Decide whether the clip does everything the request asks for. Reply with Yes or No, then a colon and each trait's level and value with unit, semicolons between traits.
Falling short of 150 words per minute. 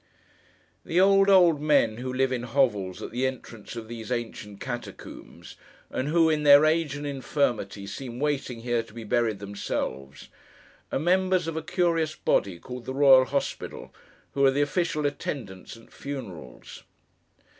No: average, 155 wpm